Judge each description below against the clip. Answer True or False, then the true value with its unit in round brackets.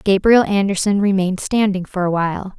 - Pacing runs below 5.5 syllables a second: False (5.6 syllables/s)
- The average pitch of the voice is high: True (195 Hz)